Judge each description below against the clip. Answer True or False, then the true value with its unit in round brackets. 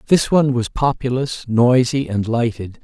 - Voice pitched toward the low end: True (125 Hz)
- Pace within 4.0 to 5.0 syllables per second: True (4.6 syllables/s)